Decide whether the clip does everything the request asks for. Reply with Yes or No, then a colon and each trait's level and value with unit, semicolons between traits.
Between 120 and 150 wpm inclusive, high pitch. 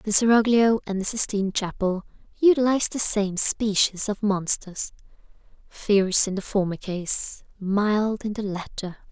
Yes: average, 140 wpm; high, 205 Hz